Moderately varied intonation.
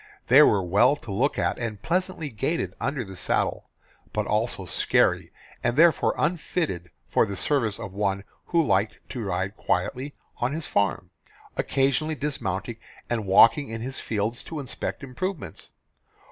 No: wide, 6.6 semitones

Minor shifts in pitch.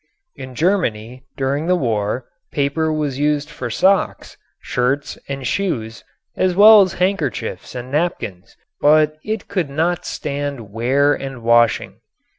No: average, 5.1 semitones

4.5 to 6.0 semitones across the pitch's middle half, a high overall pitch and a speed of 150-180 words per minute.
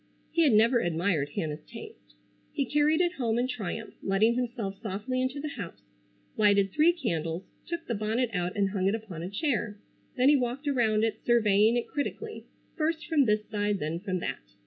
No: average, 4.9 semitones; high, 220 Hz; average, 190 wpm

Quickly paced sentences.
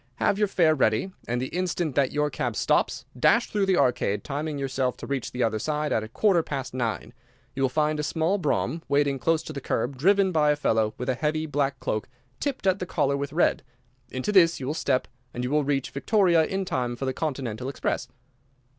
Yes: fast, 220 wpm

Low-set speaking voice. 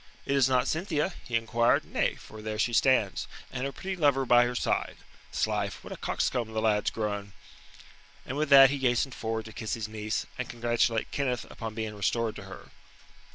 Yes: low, 120 Hz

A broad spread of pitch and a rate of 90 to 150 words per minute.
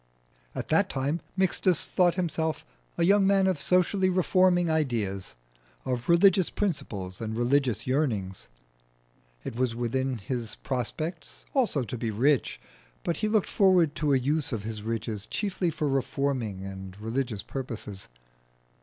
Yes: wide, 7.4 semitones; average, 140 wpm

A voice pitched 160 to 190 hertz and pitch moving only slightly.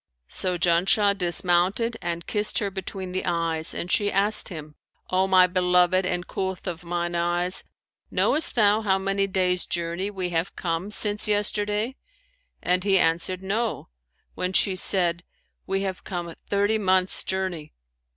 Yes: medium, 185 Hz; narrow, 2.3 semitones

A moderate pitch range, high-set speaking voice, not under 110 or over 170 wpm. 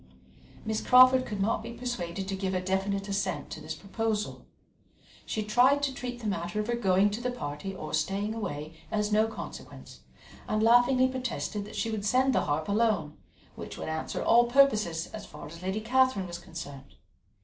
No: average, 4.3 semitones; high, 210 Hz; average, 185 wpm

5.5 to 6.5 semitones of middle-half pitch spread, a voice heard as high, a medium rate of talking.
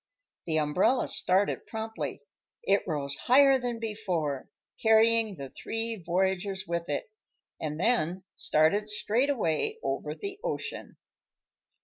No: wide, 5.9 semitones; high, 200 Hz; slow, 115 wpm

